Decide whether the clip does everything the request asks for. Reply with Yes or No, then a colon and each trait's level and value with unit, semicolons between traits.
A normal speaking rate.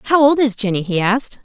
No: fast, 250 wpm